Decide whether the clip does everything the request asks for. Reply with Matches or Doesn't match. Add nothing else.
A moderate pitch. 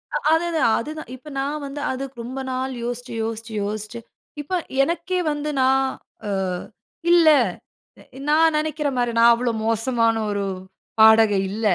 Doesn't match